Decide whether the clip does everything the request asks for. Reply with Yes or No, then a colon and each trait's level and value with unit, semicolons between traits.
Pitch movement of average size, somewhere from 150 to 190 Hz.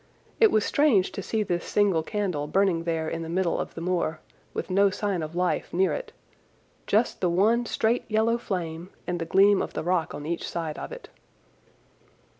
Yes: average, 3.8 semitones; medium, 185 Hz